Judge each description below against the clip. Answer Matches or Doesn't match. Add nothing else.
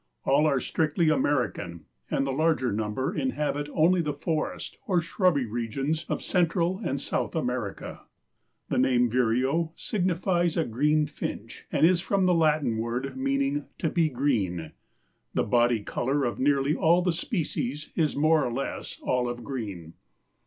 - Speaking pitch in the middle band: Matches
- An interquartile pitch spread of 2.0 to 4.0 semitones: Doesn't match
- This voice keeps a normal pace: Matches